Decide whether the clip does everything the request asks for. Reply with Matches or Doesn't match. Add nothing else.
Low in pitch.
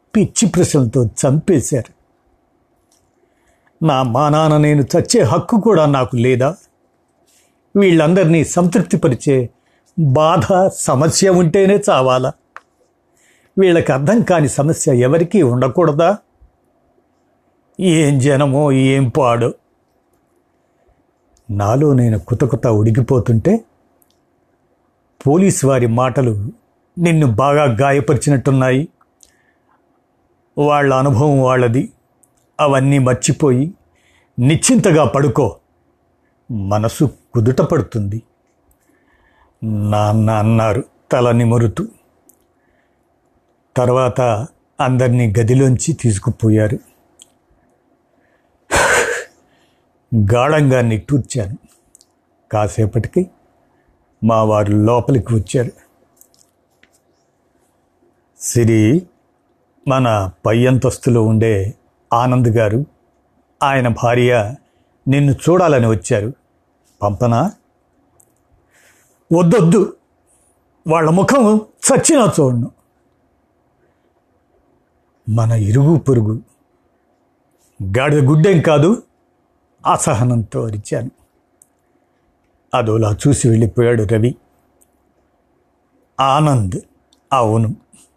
Matches